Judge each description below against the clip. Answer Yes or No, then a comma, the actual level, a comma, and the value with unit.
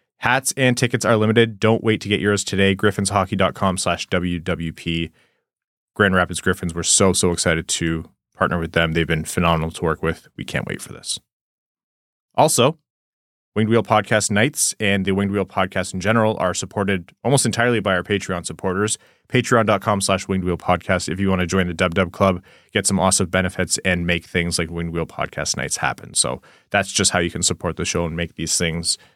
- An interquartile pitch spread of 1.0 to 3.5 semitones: Yes, average, 2.9 semitones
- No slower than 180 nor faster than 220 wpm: Yes, average, 200 wpm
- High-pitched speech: No, very low, 95 Hz